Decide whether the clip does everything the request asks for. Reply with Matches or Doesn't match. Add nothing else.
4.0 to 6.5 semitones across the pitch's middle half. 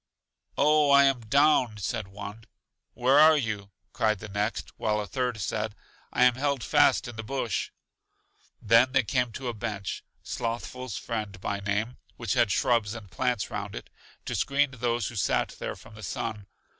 Doesn't match